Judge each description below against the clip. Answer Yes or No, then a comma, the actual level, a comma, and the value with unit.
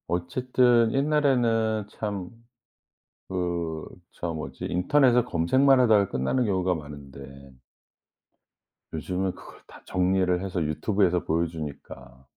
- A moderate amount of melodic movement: No, wide, 5.9 semitones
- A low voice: Yes, very low, 90 Hz